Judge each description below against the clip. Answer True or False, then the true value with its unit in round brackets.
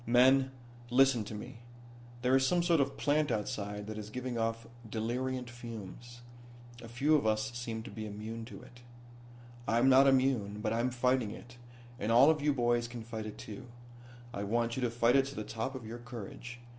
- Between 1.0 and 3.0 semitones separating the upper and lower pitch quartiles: True (2.7 semitones)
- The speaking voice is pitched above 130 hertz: False (120 Hz)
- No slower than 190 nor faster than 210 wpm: True (195 wpm)